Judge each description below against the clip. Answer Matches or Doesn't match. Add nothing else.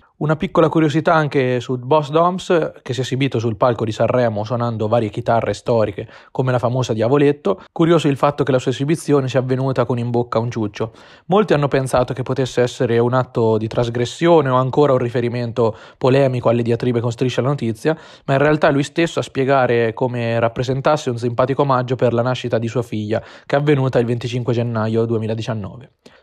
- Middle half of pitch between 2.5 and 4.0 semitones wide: Matches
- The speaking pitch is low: Matches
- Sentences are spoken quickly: Matches